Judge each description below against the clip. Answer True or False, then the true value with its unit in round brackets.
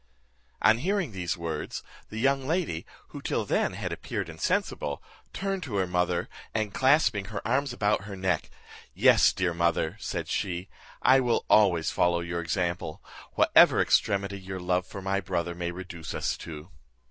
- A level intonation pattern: False (4.3 semitones)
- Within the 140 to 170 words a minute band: True (160 wpm)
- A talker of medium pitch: False (95 Hz)